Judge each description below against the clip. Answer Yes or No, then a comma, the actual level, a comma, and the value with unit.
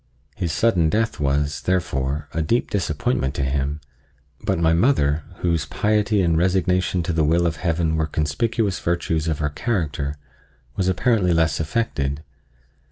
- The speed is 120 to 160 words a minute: Yes, average, 150 wpm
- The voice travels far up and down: No, average, 3.8 semitones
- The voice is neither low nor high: No, very low, 80 Hz